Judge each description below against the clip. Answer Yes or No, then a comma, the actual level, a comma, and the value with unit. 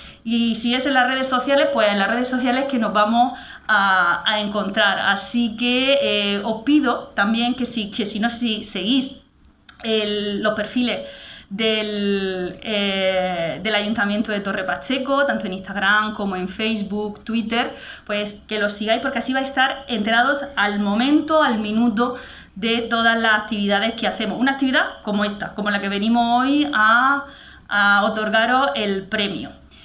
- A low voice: No, high, 220 Hz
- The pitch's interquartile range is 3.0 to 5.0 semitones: Yes, average, 3.3 semitones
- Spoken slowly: No, average, 165 wpm